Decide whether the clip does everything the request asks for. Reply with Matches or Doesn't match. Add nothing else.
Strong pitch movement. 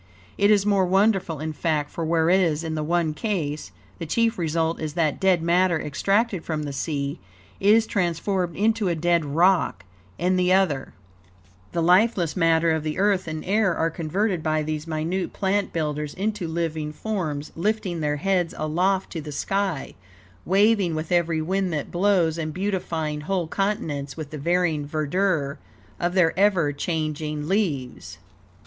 Doesn't match